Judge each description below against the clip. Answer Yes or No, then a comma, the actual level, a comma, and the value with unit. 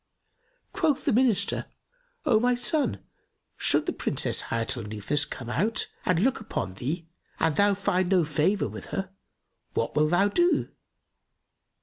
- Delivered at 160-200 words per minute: No, average, 145 wpm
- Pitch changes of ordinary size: No, wide, 7.3 semitones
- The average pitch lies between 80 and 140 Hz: No, medium, 185 Hz